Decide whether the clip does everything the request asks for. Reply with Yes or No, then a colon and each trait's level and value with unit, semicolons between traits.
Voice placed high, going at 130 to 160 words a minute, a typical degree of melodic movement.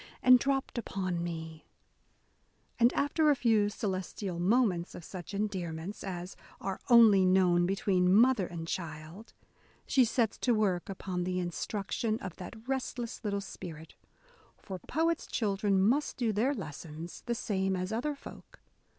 Yes: high, 195 Hz; average, 145 wpm; average, 4.5 semitones